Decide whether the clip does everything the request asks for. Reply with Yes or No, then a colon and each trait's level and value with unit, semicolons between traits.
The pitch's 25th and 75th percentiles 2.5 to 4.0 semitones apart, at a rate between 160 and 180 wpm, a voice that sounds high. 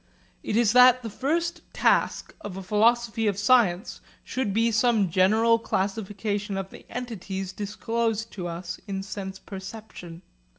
No: average, 3.1 semitones; average, 140 wpm; high, 210 Hz